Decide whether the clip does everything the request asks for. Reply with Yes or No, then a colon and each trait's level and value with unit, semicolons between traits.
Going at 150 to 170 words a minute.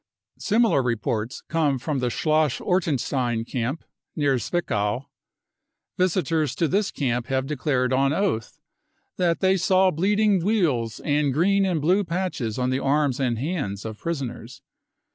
No: average, 140 wpm